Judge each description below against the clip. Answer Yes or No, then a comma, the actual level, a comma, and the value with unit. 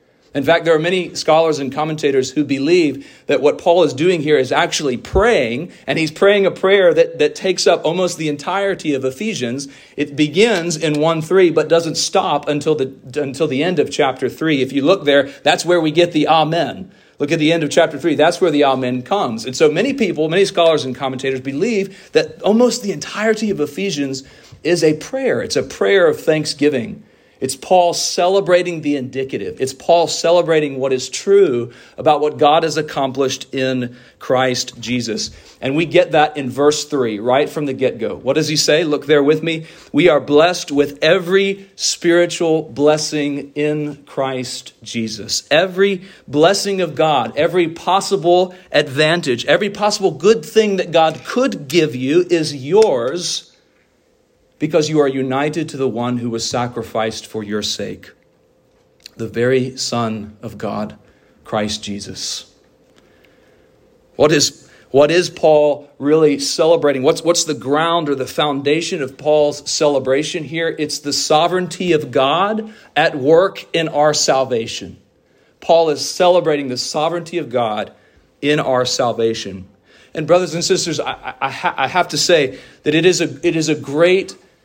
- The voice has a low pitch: No, medium, 155 Hz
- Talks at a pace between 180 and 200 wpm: No, average, 170 wpm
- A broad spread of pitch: No, average, 4.4 semitones